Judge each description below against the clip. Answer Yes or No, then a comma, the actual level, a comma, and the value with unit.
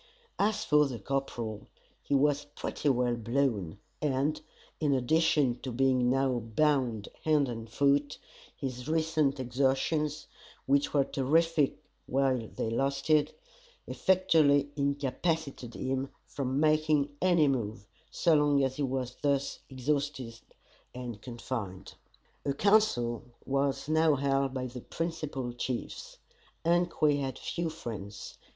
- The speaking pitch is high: No, medium, 140 Hz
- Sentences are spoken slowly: Yes, slow, 120 wpm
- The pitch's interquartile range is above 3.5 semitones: No, average, 3.1 semitones